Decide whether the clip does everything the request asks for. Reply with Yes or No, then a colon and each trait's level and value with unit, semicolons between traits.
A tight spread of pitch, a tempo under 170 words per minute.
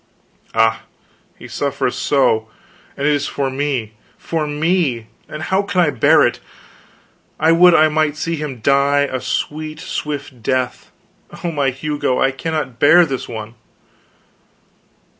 No: average, 3.2 semitones; average, 140 wpm